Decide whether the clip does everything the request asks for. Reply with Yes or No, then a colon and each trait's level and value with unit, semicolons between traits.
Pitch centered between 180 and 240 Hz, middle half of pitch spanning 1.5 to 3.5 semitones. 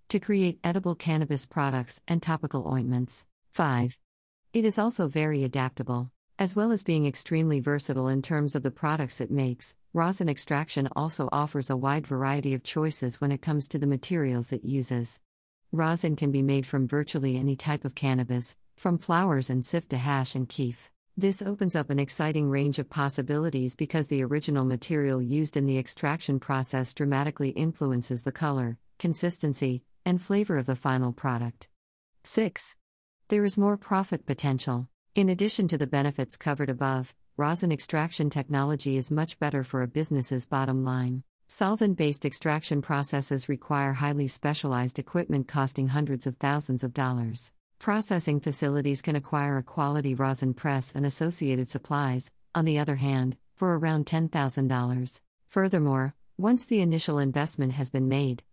No: medium, 140 Hz; average, 2.9 semitones